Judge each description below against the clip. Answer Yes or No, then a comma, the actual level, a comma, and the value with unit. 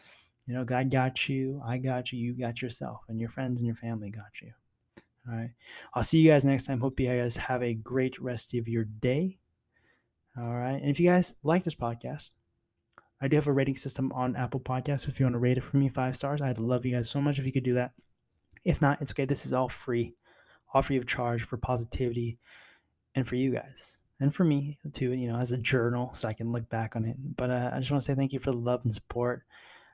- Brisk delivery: Yes, fast, 250 wpm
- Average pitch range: No, narrow, 2.3 semitones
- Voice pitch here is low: Yes, low, 125 Hz